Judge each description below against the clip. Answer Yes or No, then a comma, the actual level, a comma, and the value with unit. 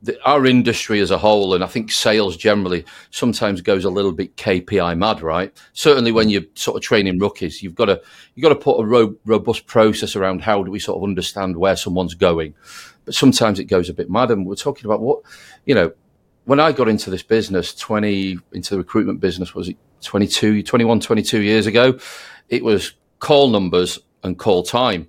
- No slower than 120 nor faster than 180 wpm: No, average, 200 wpm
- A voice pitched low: Yes, low, 100 Hz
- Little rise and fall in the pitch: No, average, 3.0 semitones